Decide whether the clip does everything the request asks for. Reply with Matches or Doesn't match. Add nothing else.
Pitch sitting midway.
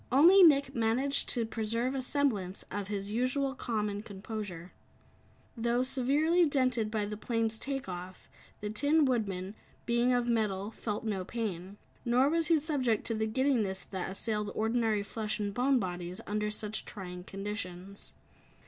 Doesn't match